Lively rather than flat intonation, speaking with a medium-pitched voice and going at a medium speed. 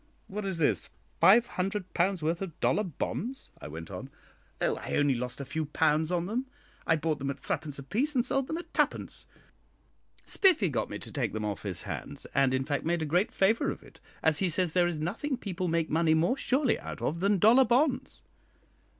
No: wide, 5.9 semitones; medium, 175 Hz; fast, 210 wpm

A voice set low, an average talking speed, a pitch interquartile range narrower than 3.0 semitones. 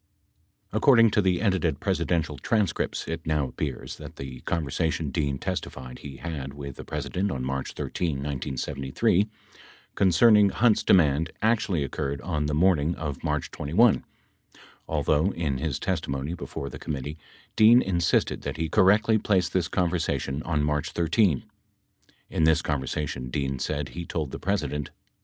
No: very low, 80 Hz; average, 150 wpm; average, 4.7 semitones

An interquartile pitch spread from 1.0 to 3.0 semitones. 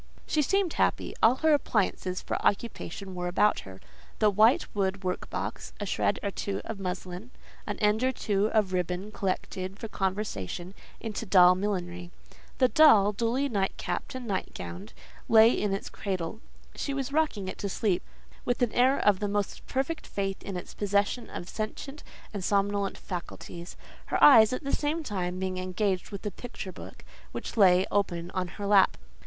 No: average, 3.5 semitones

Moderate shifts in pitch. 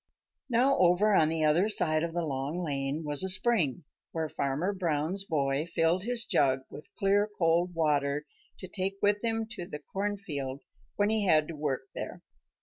Yes: average, 5.0 semitones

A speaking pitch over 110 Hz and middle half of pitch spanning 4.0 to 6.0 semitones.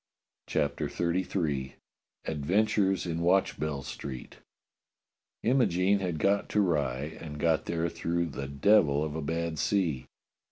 No: very low, 85 Hz; average, 4.5 semitones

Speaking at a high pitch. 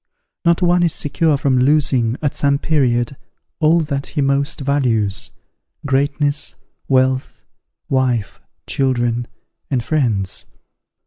No: medium, 140 Hz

